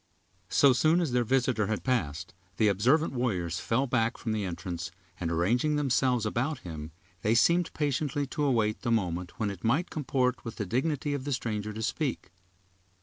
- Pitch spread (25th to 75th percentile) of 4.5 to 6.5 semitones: Yes, average, 5.1 semitones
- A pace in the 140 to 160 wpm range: No, average, 180 wpm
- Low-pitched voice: Yes, low, 120 Hz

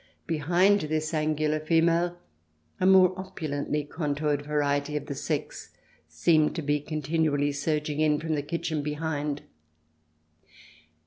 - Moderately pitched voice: Yes, medium, 150 Hz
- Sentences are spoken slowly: Yes, slow, 125 wpm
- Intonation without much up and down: Yes, narrow, 1.9 semitones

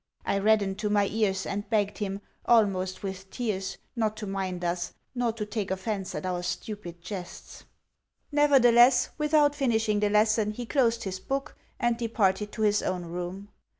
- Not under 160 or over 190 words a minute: Yes, average, 165 wpm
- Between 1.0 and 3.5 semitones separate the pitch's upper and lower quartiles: Yes, average, 3.2 semitones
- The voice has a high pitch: Yes, high, 210 Hz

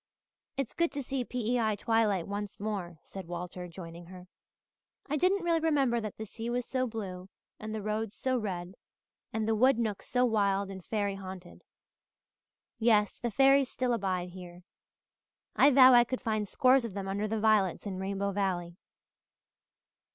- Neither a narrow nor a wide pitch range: Yes, average, 4.3 semitones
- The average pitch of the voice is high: Yes, high, 215 Hz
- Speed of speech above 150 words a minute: Yes, average, 165 wpm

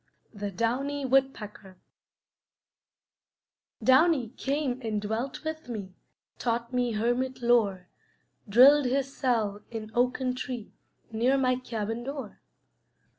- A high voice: Yes, high, 245 Hz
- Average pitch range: Yes, average, 3.2 semitones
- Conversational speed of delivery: No, slow, 105 wpm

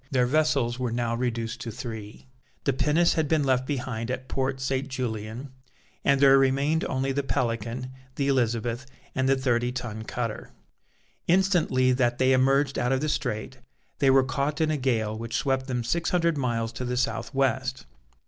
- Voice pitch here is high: No, low, 130 Hz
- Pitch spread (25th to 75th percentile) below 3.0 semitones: Yes, narrow, 2.5 semitones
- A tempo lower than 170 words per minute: No, average, 175 wpm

